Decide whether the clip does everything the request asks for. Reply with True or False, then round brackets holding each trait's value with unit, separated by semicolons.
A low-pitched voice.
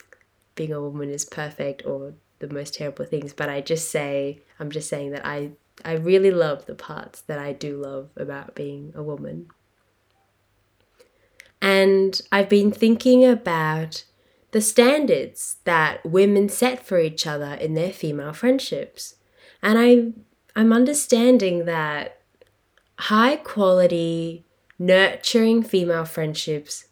False (165 Hz)